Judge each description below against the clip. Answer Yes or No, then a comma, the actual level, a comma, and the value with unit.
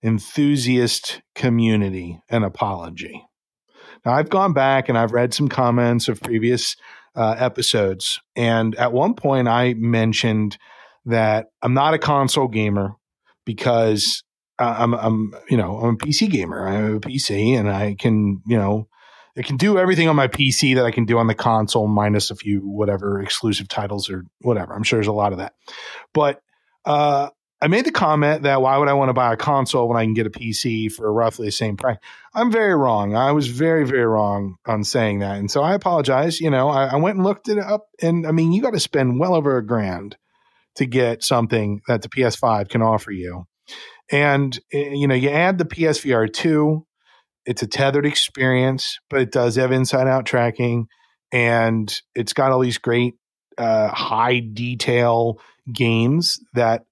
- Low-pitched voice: Yes, low, 120 Hz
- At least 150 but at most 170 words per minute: No, average, 185 wpm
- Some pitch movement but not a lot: Yes, average, 4.0 semitones